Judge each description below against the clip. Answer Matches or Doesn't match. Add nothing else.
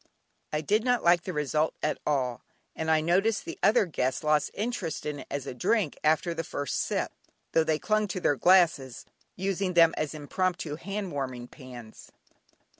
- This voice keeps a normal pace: Matches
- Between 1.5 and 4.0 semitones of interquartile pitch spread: Doesn't match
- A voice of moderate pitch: Matches